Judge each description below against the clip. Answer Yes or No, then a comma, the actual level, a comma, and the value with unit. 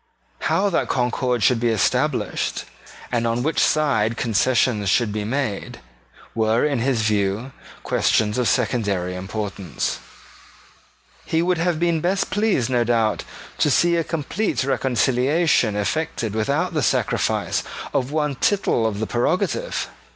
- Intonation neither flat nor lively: No, wide, 5.9 semitones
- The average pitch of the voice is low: Yes, low, 125 Hz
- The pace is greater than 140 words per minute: No, slow, 135 wpm